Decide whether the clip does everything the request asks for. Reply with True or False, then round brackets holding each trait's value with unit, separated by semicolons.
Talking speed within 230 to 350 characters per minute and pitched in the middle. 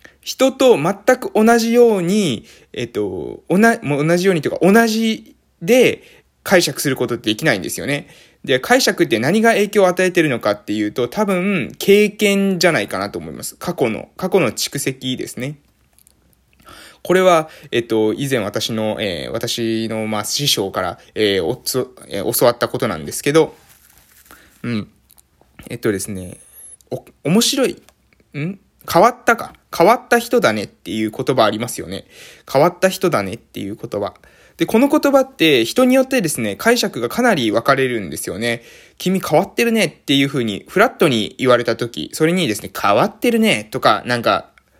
True (335 characters per minute; 170 Hz)